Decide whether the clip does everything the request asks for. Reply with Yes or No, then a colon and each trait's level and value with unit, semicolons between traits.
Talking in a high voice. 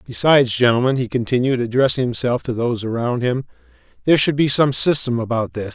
No: low, 125 Hz